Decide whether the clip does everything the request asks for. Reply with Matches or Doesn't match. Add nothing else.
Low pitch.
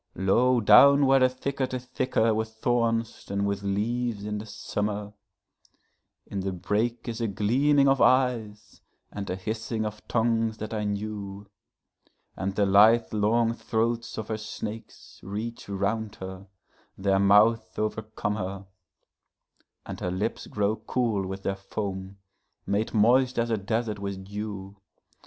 Matches